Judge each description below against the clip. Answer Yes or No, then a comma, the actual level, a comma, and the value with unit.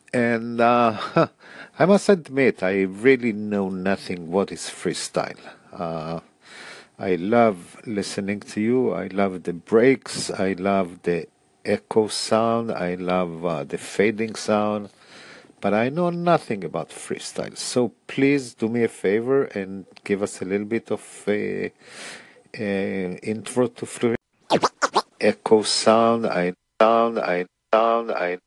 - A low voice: Yes, low, 105 Hz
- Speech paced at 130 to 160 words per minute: Yes, slow, 135 wpm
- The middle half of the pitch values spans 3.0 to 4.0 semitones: Yes, average, 3.5 semitones